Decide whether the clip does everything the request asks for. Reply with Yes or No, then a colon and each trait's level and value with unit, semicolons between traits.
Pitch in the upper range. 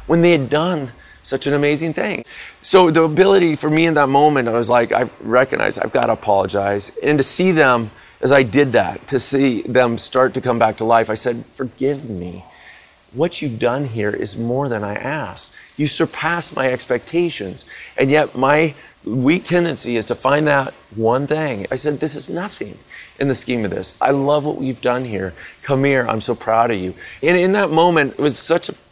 No: low, 135 Hz